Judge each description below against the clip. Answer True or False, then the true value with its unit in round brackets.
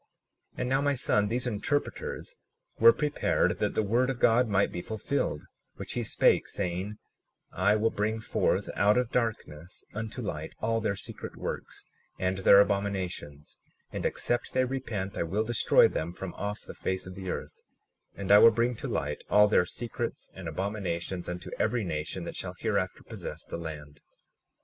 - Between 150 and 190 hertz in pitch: False (105 Hz)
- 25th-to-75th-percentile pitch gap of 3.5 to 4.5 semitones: True (4.0 semitones)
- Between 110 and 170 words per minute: False (180 wpm)